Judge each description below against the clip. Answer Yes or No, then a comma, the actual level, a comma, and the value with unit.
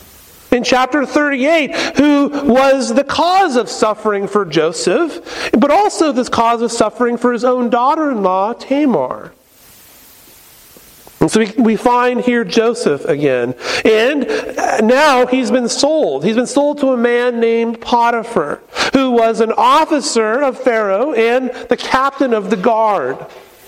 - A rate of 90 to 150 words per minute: Yes, average, 140 wpm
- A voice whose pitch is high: Yes, high, 245 Hz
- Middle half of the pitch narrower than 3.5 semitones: Yes, average, 2.9 semitones